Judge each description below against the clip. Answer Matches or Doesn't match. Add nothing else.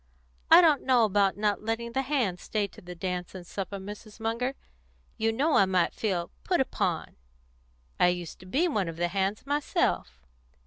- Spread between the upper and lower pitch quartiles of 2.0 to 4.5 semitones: Doesn't match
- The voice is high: Matches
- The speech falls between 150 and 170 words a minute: Doesn't match